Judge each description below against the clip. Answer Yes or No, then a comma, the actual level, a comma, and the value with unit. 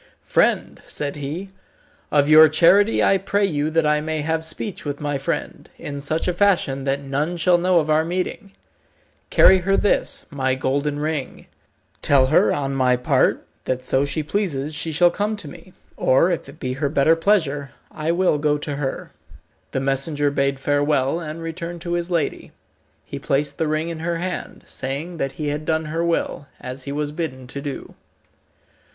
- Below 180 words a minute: No, average, 185 wpm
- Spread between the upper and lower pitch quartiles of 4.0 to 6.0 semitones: No, average, 3.3 semitones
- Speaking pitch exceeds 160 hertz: No, medium, 150 Hz